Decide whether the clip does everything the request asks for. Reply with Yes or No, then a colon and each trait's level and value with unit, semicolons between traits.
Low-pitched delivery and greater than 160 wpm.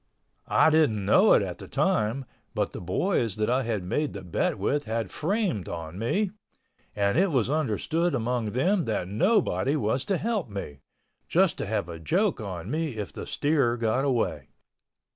Yes: low, 125 Hz; average, 170 wpm